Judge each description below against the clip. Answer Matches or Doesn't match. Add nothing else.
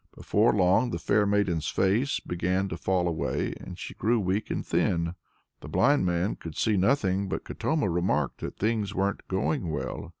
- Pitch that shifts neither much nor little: Matches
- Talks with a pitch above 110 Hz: Doesn't match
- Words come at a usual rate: Matches